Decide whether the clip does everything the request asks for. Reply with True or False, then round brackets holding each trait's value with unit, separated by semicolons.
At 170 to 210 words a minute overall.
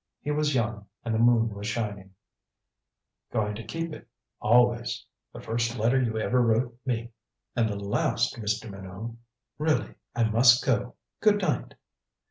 False (160 wpm)